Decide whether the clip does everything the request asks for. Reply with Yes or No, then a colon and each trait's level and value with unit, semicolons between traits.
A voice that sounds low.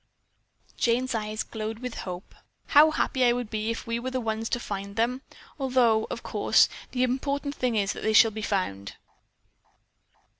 No: high, 230 Hz